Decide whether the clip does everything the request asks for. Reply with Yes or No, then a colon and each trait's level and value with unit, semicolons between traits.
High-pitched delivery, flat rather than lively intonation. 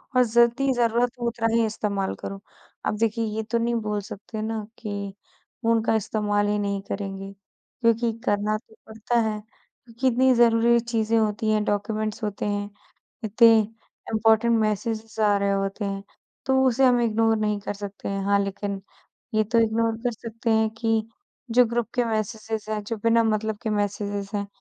Yes: high, 220 Hz; narrow, 2.0 semitones